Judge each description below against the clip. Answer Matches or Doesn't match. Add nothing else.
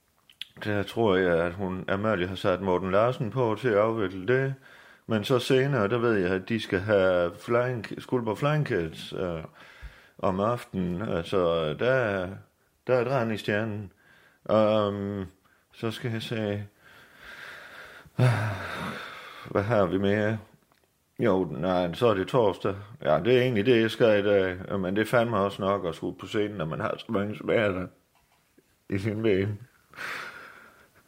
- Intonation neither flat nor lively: Matches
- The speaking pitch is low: Matches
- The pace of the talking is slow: Doesn't match